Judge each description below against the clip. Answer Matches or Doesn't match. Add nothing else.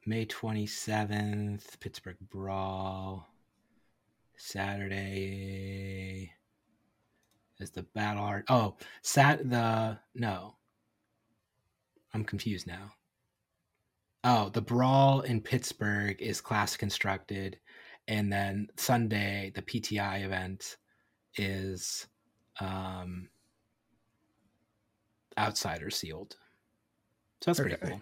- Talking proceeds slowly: Matches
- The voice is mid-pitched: Doesn't match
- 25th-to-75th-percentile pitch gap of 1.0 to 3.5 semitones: Matches